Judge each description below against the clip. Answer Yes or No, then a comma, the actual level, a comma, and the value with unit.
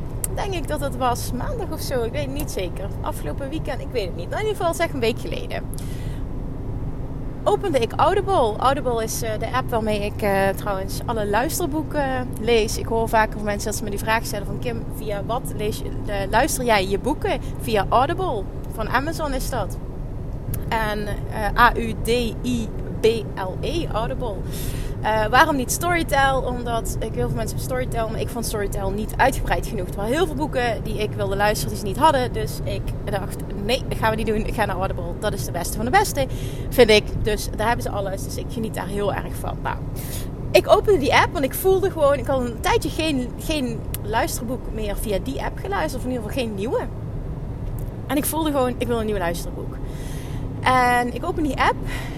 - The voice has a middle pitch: No, high, 205 Hz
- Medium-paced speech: No, fast, 205 wpm